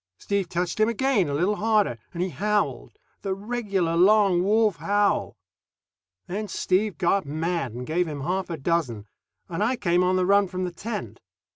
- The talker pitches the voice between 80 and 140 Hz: No, medium, 185 Hz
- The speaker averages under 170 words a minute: No, average, 175 wpm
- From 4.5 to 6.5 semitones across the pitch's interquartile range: No, average, 3.5 semitones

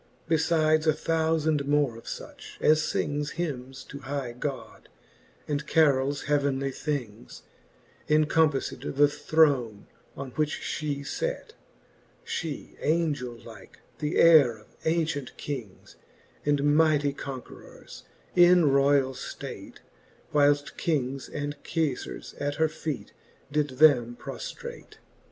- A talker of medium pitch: Yes, medium, 145 Hz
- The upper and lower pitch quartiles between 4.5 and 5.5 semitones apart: No, narrow, 2.5 semitones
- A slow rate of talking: Yes, slow, 110 wpm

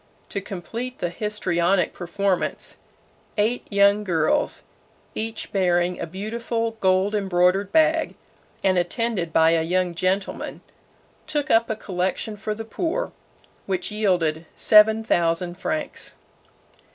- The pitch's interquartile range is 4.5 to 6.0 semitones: No, average, 3.9 semitones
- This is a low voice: No, high, 195 Hz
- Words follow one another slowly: Yes, slow, 115 wpm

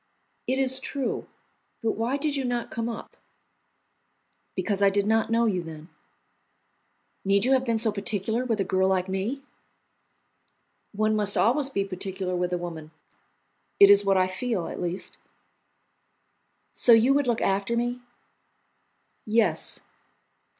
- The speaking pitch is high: Yes, high, 215 Hz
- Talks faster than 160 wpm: No, average, 145 wpm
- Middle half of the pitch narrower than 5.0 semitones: Yes, average, 4.0 semitones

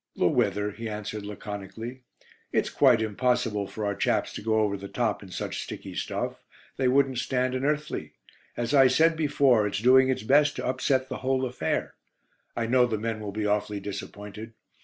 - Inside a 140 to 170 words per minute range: No, average, 185 wpm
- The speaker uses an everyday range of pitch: Yes, average, 3.9 semitones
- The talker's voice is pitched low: Yes, low, 115 Hz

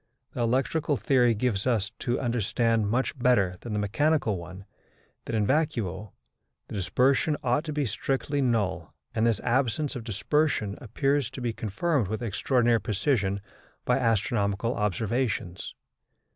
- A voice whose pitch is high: No, low, 115 Hz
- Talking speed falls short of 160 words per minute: Yes, average, 140 wpm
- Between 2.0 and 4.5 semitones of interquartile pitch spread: Yes, average, 4.2 semitones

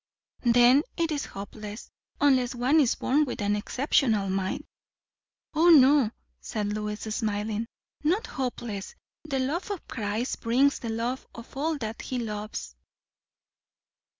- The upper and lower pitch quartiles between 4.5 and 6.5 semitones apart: Yes, average, 4.9 semitones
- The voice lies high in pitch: Yes, high, 240 Hz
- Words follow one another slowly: Yes, slow, 130 wpm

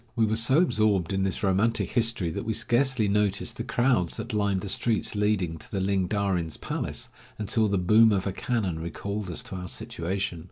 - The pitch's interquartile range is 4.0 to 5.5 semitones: No, average, 3.0 semitones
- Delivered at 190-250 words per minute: Yes, average, 200 wpm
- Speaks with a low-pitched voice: Yes, low, 100 Hz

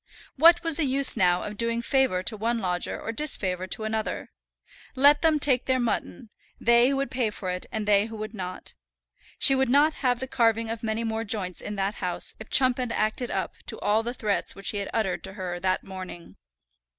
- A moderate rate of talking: No, fast, 210 wpm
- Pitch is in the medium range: No, high, 225 Hz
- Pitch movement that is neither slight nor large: Yes, average, 4.5 semitones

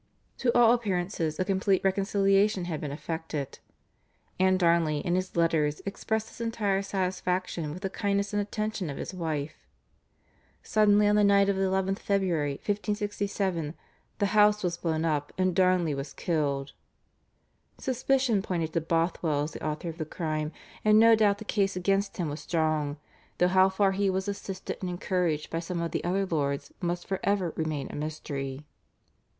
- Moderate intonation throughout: Yes, average, 3.9 semitones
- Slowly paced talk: No, average, 170 wpm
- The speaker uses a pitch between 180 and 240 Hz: Yes, medium, 185 Hz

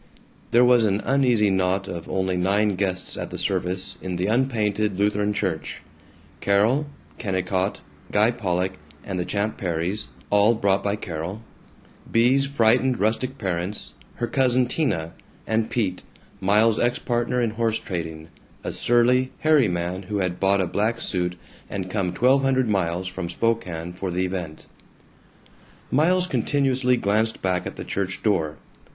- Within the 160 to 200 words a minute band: No, average, 150 wpm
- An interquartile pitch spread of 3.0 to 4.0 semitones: No, average, 4.4 semitones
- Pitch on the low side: Yes, low, 100 Hz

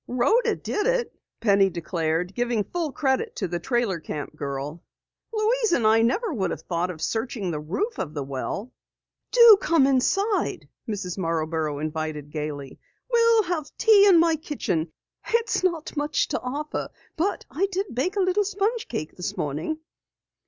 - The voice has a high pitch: Yes, high, 245 Hz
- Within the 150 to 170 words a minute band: Yes, average, 160 wpm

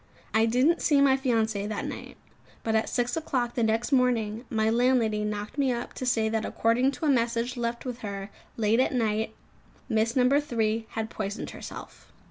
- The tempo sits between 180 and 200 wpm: Yes, average, 185 wpm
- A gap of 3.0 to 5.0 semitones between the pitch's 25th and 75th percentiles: No, narrow, 2.4 semitones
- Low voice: No, high, 230 Hz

